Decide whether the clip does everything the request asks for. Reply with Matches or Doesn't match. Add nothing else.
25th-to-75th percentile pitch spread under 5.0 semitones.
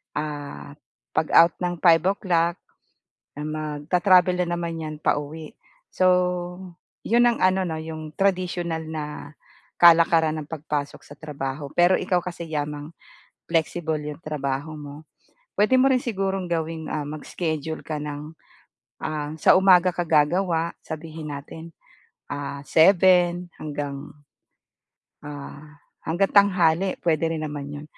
Matches